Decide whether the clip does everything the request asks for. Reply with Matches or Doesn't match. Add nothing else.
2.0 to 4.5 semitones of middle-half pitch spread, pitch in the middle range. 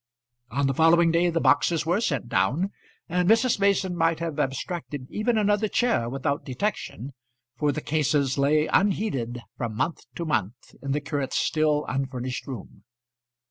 Doesn't match